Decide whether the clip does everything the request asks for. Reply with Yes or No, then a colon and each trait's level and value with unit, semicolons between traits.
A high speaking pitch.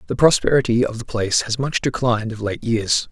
No: low, 115 Hz